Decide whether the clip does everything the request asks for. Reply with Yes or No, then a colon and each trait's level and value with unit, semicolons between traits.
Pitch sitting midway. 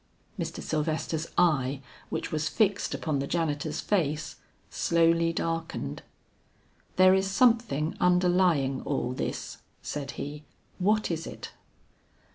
Yes: medium, 165 Hz